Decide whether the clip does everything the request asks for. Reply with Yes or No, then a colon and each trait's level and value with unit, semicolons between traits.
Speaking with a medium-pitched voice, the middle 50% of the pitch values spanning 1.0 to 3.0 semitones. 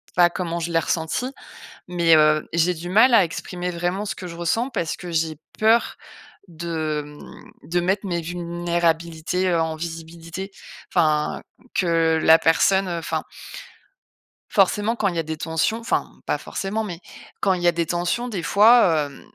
Yes: medium, 170 Hz; average, 2.7 semitones